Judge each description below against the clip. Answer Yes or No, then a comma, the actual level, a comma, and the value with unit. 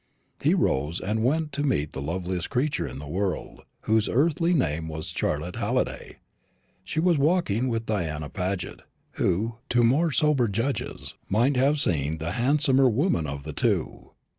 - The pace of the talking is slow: No, average, 160 wpm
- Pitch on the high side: No, low, 110 Hz